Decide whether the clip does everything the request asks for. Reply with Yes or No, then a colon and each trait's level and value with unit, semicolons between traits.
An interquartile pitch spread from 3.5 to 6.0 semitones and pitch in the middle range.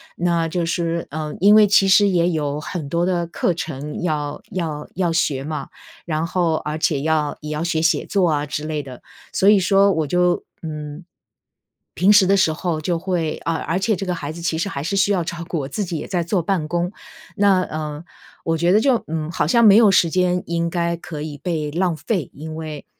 No: average, 2.9 semitones; medium, 170 Hz